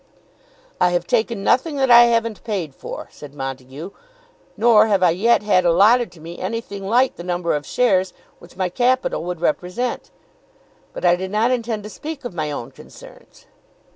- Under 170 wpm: No, average, 175 wpm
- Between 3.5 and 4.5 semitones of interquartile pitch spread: No, average, 5.1 semitones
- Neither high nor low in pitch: No, high, 195 Hz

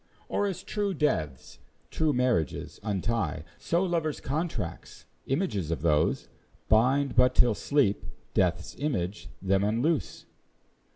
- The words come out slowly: Yes, slow, 115 wpm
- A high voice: No, low, 125 Hz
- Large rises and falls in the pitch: Yes, wide, 8.5 semitones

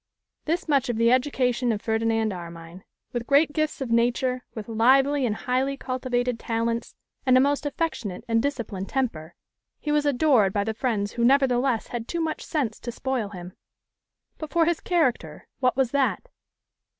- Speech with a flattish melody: No, average, 3.7 semitones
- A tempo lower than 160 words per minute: No, average, 170 wpm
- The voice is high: Yes, very high, 250 Hz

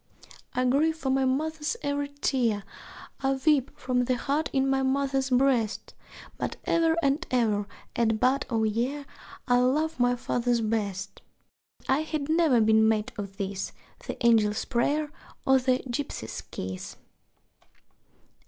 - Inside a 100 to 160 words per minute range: Yes, average, 145 wpm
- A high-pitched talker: Yes, very high, 260 Hz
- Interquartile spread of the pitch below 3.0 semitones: No, average, 3.9 semitones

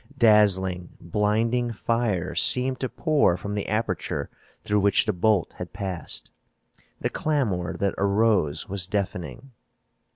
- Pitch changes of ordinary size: Yes, average, 3.8 semitones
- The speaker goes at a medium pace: No, slow, 125 wpm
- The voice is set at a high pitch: No, low, 105 Hz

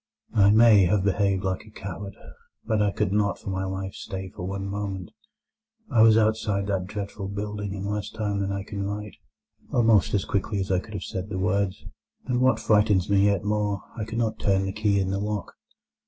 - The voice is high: No, low, 100 Hz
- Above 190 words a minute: Yes, average, 200 wpm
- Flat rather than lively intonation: Yes, narrow, 1.5 semitones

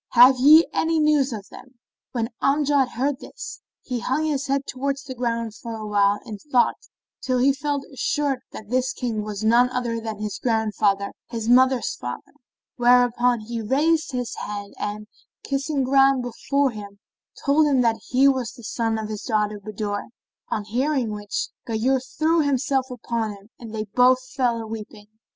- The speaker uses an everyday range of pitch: Yes, average, 3.8 semitones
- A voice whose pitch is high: Yes, high, 245 Hz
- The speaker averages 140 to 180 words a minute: Yes, average, 175 wpm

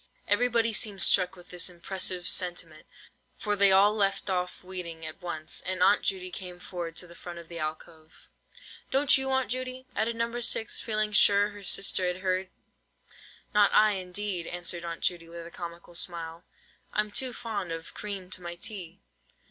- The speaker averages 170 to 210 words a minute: Yes, average, 175 wpm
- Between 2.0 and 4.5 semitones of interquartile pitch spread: Yes, average, 3.3 semitones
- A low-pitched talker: No, medium, 185 Hz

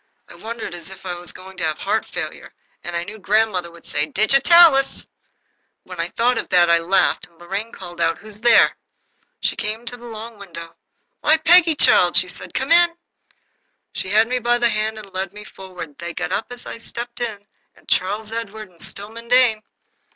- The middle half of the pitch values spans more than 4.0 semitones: Yes, average, 4.7 semitones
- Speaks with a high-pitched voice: Yes, high, 210 Hz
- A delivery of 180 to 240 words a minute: Yes, average, 195 wpm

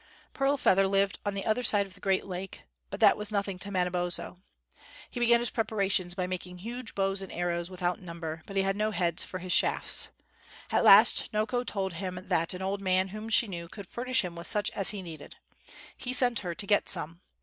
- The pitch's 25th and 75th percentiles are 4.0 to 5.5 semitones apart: No, average, 2.7 semitones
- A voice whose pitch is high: Yes, high, 195 Hz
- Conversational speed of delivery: No, fast, 215 wpm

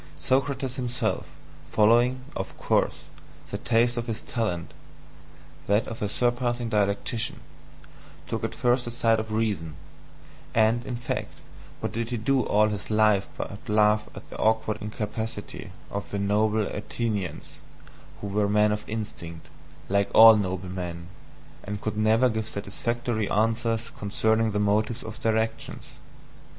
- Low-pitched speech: Yes, low, 110 Hz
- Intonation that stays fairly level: Yes, narrow, 2.1 semitones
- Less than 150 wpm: Yes, average, 140 wpm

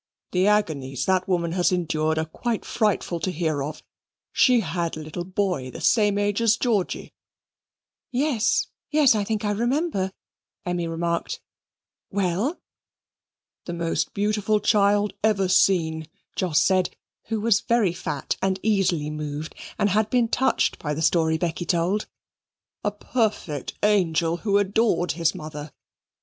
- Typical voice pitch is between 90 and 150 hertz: No, medium, 185 Hz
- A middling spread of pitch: Yes, average, 4.3 semitones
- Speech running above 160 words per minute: No, average, 145 wpm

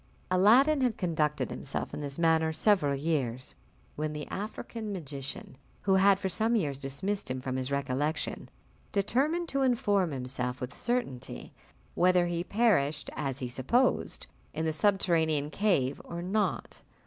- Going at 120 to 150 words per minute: Yes, average, 145 wpm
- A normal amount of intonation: No, wide, 6.6 semitones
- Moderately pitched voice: Yes, medium, 165 Hz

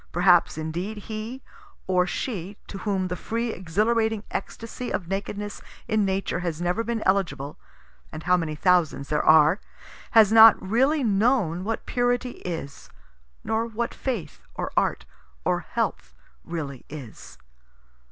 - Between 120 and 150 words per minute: Yes, slow, 135 wpm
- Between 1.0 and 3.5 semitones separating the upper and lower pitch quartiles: No, average, 5.0 semitones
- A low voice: No, high, 195 Hz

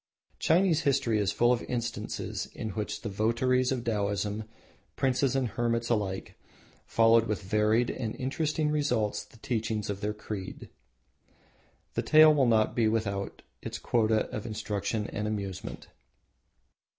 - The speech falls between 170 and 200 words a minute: No, average, 140 wpm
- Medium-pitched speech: No, low, 115 Hz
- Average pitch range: Yes, average, 3.0 semitones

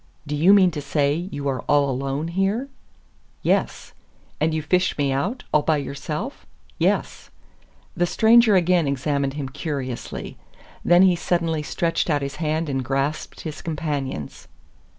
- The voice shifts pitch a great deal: No, average, 3.9 semitones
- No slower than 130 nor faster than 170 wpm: Yes, average, 150 wpm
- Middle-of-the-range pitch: Yes, medium, 150 Hz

